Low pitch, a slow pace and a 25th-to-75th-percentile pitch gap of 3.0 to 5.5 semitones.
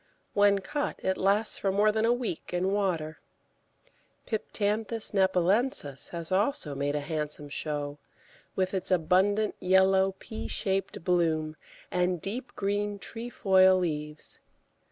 No: high, 190 Hz; slow, 125 wpm; average, 3.9 semitones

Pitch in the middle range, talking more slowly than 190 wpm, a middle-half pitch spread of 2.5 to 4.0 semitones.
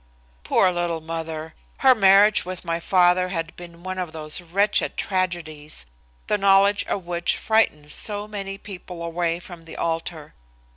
Yes: medium, 175 Hz; average, 150 wpm; average, 2.9 semitones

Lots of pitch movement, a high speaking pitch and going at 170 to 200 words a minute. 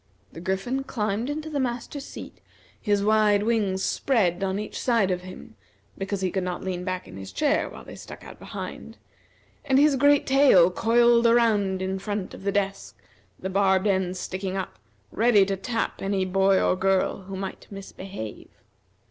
No: average, 3.7 semitones; high, 195 Hz; average, 175 wpm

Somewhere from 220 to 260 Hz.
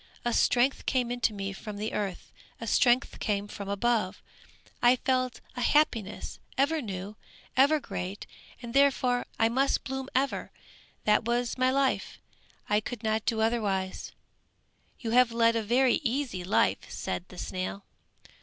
Yes: high, 235 Hz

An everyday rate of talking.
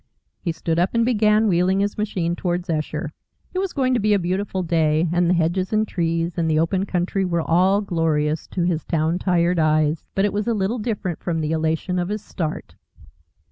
No: fast, 210 wpm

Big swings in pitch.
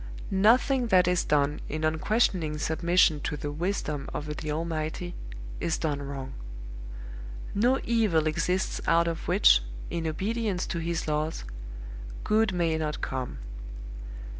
No: average, 3.7 semitones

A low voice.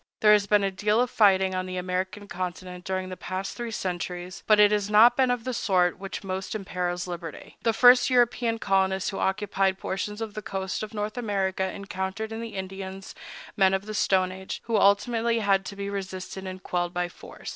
No: high, 195 Hz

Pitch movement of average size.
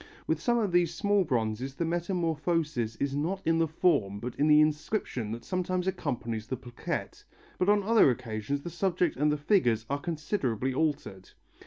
No: wide, 6.1 semitones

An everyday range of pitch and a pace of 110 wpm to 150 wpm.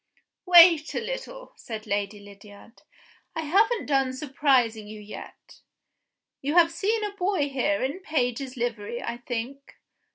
No: wide, 6.7 semitones; average, 140 wpm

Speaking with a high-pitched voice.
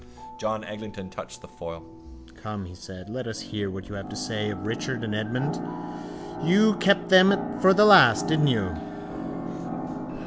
No: low, 110 Hz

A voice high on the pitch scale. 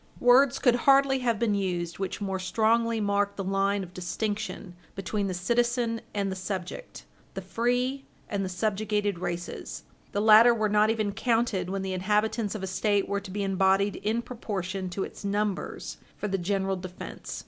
Yes: high, 205 Hz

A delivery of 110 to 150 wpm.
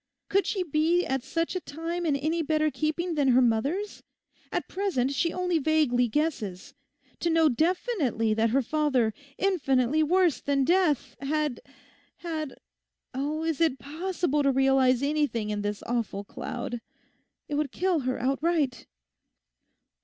Yes: average, 140 wpm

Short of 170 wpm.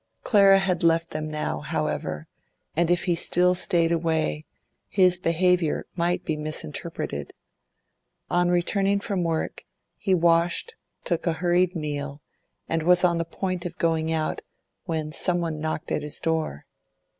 Yes: average, 145 wpm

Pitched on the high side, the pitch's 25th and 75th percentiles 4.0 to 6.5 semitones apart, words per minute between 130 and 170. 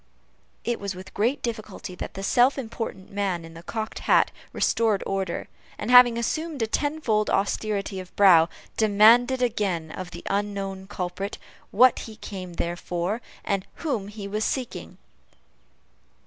No: high, 205 Hz; average, 3.4 semitones; average, 150 wpm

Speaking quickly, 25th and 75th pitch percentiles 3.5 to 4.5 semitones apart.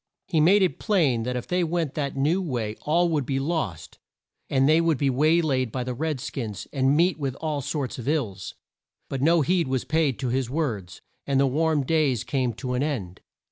Yes: fast, 215 wpm; average, 4.1 semitones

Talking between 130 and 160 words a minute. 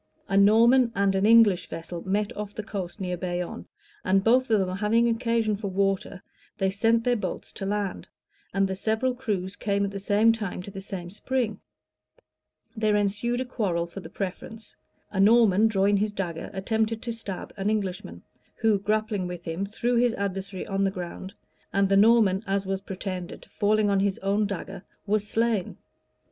No: average, 180 wpm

